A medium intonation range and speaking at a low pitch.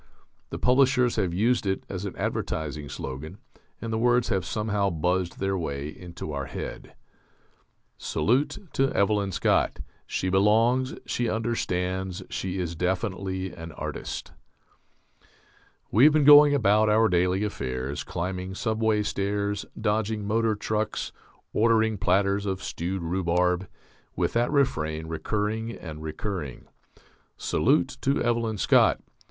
Yes: average, 3.9 semitones; low, 100 Hz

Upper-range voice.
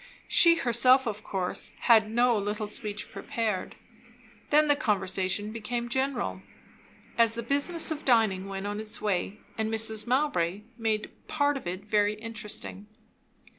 Yes: high, 220 Hz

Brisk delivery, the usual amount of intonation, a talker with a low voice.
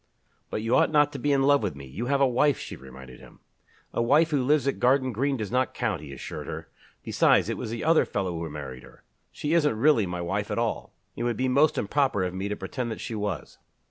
No: fast, 250 wpm; wide, 6.7 semitones; low, 120 Hz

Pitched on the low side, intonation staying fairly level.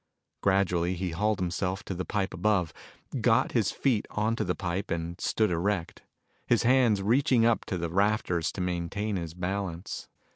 No: very low, 95 Hz; average, 3.5 semitones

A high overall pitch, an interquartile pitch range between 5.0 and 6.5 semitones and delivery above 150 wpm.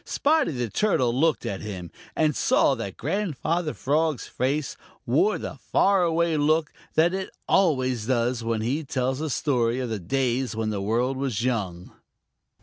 No: low, 130 Hz; wide, 5.4 semitones; average, 160 wpm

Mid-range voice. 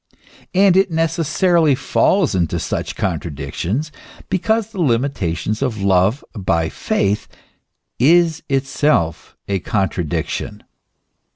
No: low, 130 Hz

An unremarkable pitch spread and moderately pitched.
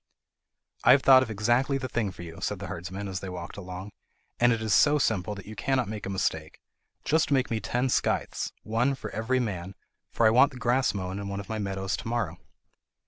No: average, 4.5 semitones; low, 110 Hz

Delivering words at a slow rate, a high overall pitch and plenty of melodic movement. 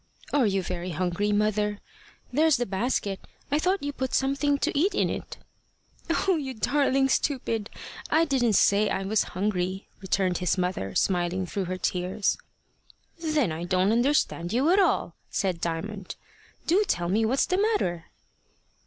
No: average, 155 wpm; high, 210 Hz; wide, 7.3 semitones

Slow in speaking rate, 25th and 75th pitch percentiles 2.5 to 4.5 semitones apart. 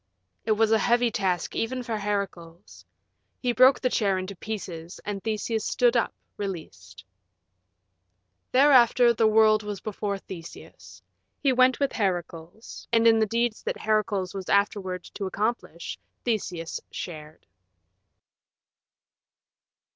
Yes: slow, 125 wpm; average, 3.8 semitones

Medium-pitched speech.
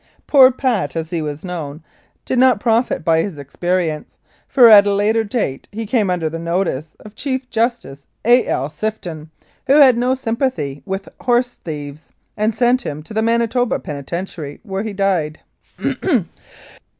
No: high, 200 Hz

